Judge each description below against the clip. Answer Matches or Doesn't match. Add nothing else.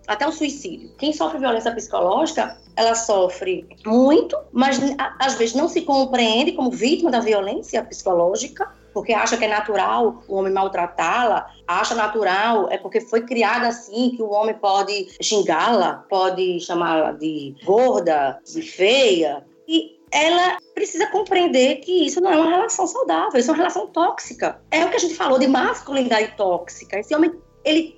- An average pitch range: Doesn't match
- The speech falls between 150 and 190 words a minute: Matches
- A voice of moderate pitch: Doesn't match